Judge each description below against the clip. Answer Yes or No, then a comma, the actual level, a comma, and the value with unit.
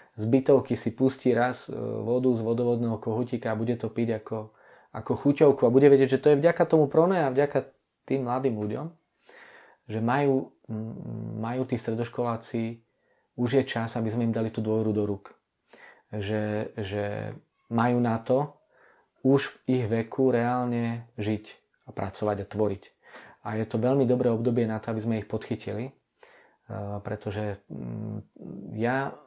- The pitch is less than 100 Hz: No, low, 115 Hz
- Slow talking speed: No, average, 155 wpm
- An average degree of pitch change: Yes, average, 3.1 semitones